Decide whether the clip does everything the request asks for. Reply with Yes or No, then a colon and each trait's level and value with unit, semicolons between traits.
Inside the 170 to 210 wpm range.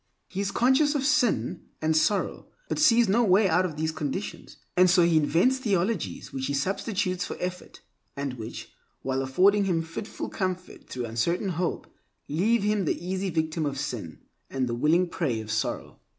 Yes: average, 180 wpm